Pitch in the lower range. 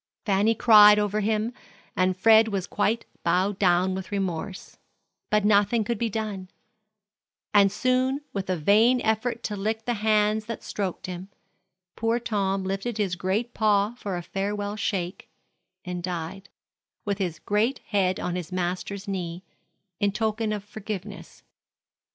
No: high, 205 Hz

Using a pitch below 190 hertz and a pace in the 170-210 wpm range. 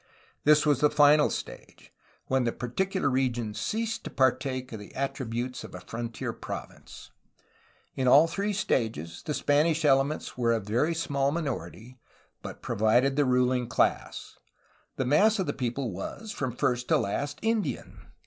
No: low, 135 Hz; average, 155 wpm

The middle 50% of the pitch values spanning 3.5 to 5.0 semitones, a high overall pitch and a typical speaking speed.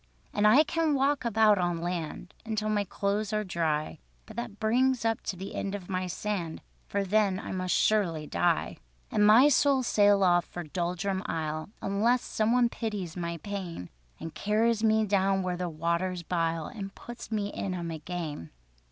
Yes: average, 3.8 semitones; high, 195 Hz; average, 180 wpm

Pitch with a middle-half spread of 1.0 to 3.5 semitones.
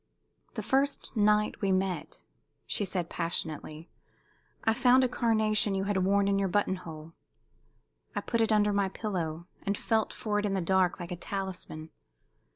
Yes: average, 3.0 semitones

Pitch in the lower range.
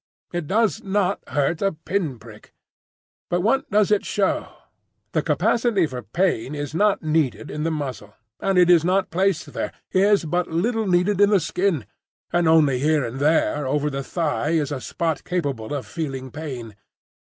No: medium, 160 Hz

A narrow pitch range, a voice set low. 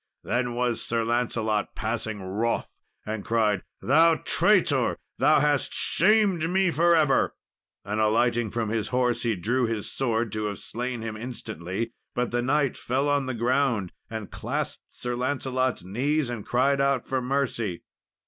No: average, 3.5 semitones; low, 120 Hz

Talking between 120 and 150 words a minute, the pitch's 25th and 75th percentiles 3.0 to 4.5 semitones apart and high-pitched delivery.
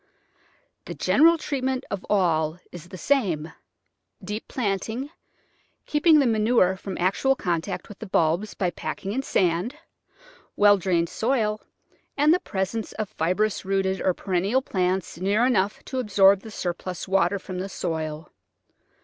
Yes: average, 140 wpm; average, 4.1 semitones; high, 195 Hz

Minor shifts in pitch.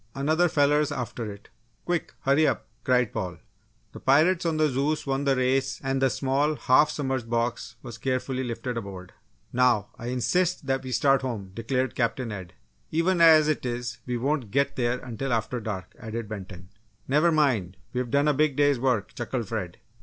No: average, 3.7 semitones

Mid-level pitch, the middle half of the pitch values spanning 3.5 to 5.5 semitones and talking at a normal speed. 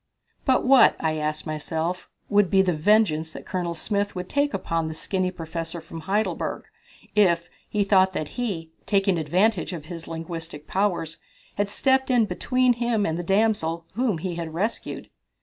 Yes: medium, 180 Hz; average, 4.3 semitones; average, 165 wpm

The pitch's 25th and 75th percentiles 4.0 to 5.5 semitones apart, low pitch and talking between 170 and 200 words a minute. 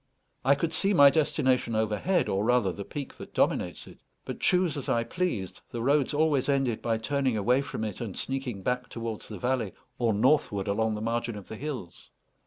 Yes: average, 4.3 semitones; low, 125 Hz; average, 195 wpm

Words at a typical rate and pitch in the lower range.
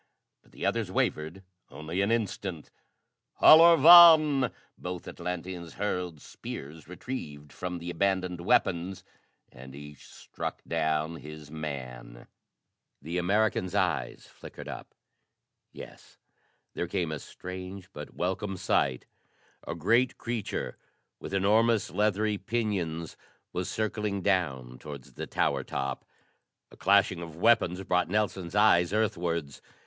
No: slow, 120 wpm; very low, 90 Hz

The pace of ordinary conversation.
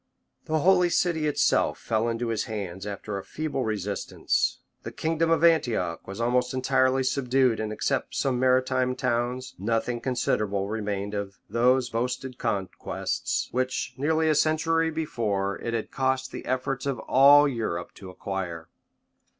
Yes: average, 150 wpm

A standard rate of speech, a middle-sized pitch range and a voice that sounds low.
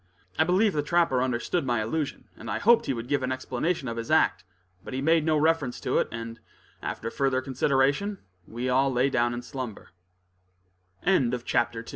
Yes: average, 175 wpm; average, 4.5 semitones; low, 130 Hz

